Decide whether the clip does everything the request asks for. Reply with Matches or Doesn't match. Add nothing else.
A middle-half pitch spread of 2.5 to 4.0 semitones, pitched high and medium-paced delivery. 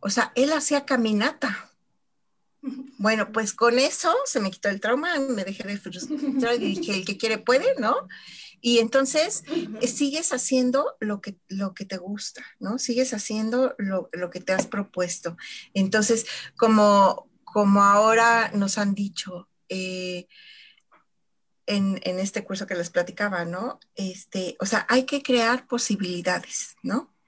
Doesn't match